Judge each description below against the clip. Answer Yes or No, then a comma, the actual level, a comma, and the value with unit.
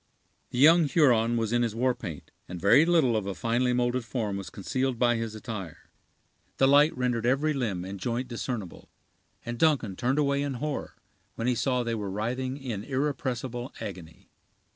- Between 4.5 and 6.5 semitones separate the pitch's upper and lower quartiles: No, average, 3.3 semitones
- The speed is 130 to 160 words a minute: No, average, 180 wpm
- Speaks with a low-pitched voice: Yes, low, 120 Hz